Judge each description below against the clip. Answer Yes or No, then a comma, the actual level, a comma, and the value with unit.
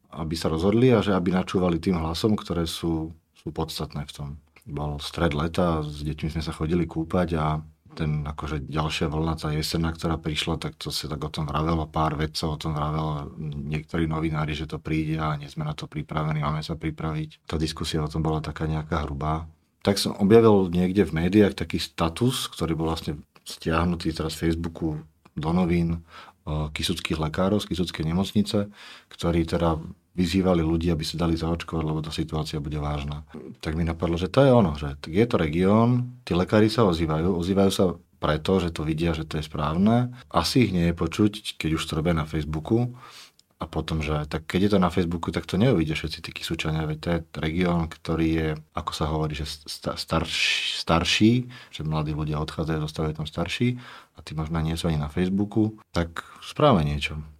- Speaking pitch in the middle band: No, very low, 80 Hz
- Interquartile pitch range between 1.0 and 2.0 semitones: No, narrow, 2.4 semitones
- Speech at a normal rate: No, fast, 190 wpm